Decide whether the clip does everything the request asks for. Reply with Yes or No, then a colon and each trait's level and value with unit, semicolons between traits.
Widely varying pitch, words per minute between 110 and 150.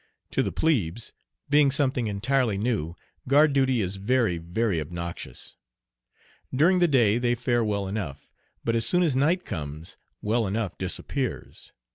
Yes: wide, 5.9 semitones; average, 145 wpm